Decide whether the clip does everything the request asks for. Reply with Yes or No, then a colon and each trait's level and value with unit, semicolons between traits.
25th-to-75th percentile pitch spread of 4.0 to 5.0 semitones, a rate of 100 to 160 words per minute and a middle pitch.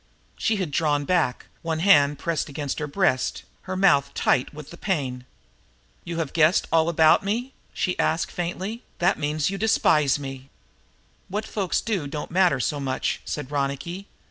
No: average, 4.6 semitones; average, 170 wpm; medium, 160 Hz